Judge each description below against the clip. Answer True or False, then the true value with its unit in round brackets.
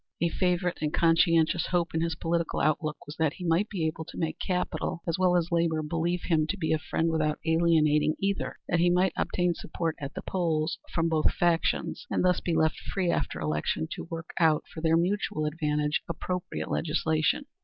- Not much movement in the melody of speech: True (1.8 semitones)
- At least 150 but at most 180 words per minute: False (195 wpm)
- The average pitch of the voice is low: False (165 Hz)